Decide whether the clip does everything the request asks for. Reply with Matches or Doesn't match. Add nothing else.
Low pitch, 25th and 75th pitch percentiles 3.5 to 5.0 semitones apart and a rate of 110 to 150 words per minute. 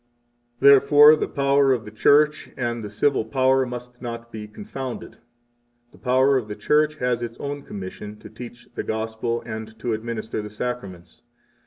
Doesn't match